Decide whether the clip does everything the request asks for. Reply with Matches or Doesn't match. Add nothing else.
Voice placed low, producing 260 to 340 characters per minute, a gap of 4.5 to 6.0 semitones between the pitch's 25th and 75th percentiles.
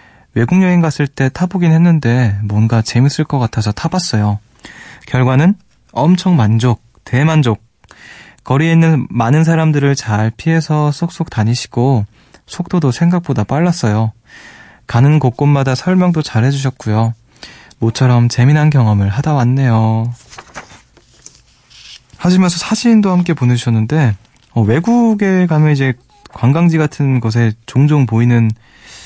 Matches